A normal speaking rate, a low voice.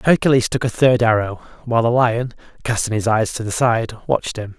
No: fast, 210 wpm; low, 115 Hz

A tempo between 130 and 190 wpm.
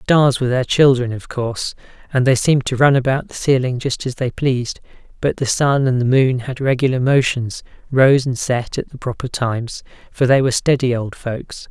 No: fast, 205 wpm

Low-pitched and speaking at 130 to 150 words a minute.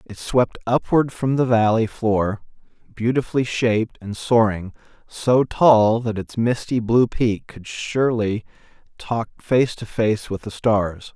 Yes: low, 115 Hz; average, 145 wpm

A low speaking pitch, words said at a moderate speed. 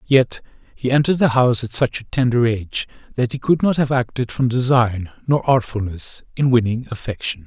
Yes: low, 120 Hz; average, 185 wpm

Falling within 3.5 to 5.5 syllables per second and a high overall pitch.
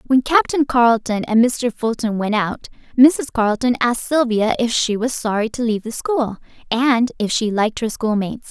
Yes: 5.3 syllables/s; high, 235 Hz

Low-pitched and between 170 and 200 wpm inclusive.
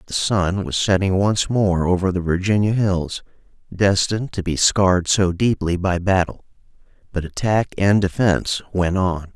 No: very low, 95 Hz; average, 155 wpm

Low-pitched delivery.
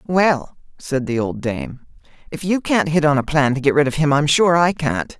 No: medium, 145 Hz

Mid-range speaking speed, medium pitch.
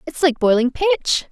No: average, 185 wpm; very high, 265 Hz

